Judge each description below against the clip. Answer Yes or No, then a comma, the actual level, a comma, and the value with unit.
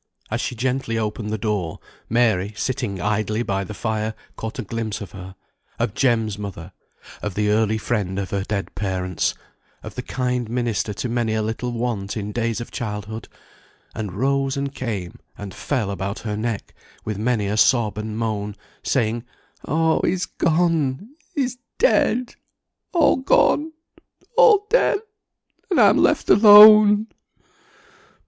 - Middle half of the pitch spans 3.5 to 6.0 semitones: Yes, average, 4.1 semitones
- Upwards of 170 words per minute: No, average, 150 wpm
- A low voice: Yes, low, 110 Hz